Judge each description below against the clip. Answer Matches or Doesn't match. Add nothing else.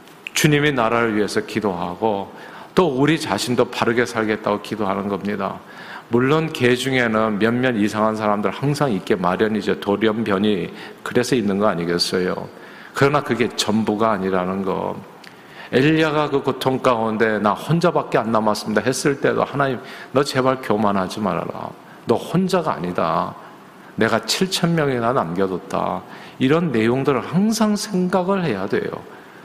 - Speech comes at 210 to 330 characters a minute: Matches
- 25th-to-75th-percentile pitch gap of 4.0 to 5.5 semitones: Matches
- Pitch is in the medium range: Doesn't match